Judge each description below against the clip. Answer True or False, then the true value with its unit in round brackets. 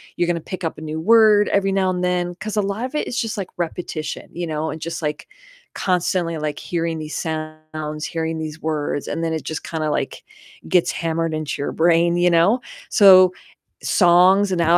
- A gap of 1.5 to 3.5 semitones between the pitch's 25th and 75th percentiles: True (2.8 semitones)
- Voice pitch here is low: False (170 Hz)